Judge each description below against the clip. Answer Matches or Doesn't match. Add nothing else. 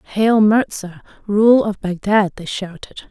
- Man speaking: Doesn't match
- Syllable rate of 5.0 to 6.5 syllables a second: Doesn't match